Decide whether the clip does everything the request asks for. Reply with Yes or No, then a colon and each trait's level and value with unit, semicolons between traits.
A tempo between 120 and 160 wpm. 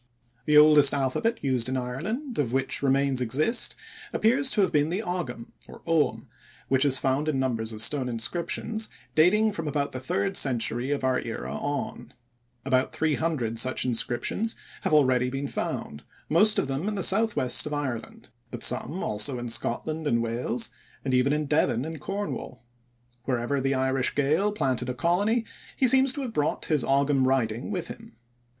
No: average, 170 wpm